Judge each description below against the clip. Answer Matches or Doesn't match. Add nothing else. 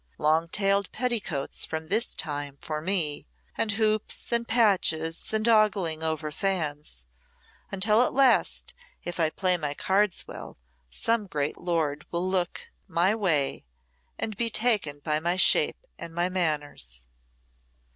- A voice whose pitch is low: Doesn't match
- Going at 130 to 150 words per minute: Matches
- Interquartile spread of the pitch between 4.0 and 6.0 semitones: Matches